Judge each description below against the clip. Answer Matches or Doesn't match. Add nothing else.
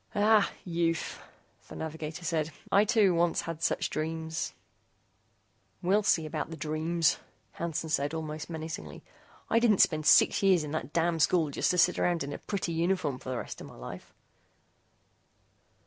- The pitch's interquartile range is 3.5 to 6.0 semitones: Doesn't match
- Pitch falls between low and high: Matches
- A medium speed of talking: Matches